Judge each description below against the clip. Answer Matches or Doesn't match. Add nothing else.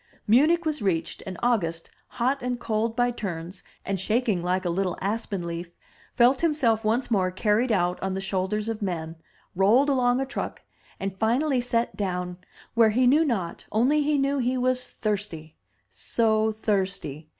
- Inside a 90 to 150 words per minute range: Doesn't match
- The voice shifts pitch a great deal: Doesn't match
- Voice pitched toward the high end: Matches